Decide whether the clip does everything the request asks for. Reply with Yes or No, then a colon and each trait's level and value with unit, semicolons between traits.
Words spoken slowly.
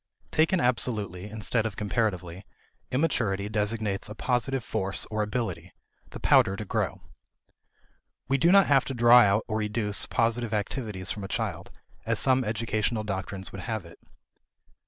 No: average, 150 wpm